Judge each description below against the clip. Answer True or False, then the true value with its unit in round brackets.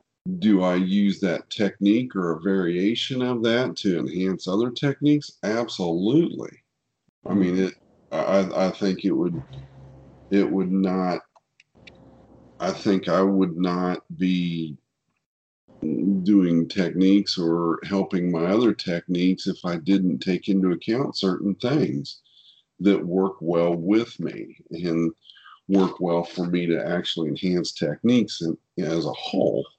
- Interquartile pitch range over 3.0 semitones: False (2.7 semitones)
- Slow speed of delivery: True (130 wpm)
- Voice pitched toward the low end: True (95 Hz)